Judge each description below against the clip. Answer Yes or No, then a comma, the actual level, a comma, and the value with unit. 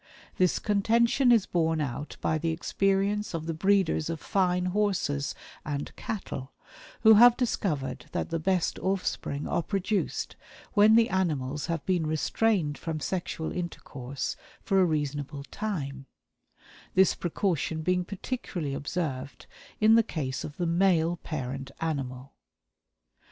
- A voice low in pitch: No, medium, 170 Hz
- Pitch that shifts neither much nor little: Yes, average, 5.0 semitones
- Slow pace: Yes, slow, 130 wpm